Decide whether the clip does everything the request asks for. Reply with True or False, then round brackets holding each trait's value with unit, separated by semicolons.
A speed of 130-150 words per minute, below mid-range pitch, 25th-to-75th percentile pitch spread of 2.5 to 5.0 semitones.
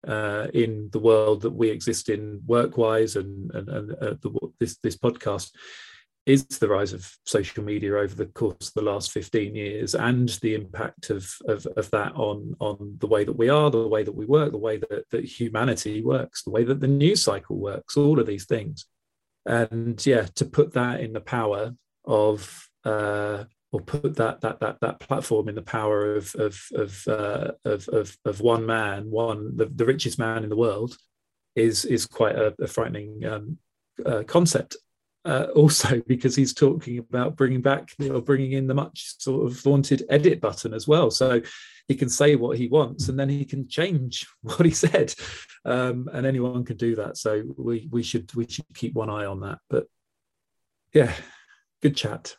False (195 wpm; 115 Hz; 4.2 semitones)